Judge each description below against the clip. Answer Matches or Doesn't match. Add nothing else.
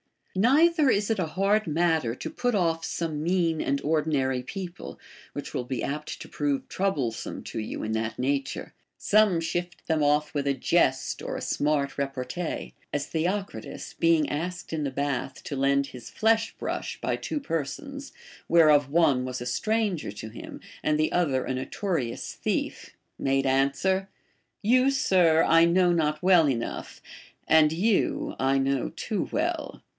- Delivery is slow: Doesn't match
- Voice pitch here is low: Doesn't match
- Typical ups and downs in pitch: Matches